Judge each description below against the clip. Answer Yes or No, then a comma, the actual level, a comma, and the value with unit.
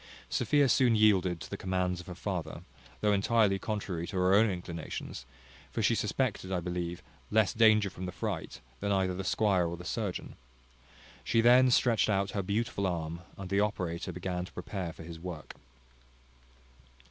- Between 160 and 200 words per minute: Yes, average, 170 wpm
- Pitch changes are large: No, average, 3.2 semitones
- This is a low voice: Yes, very low, 95 Hz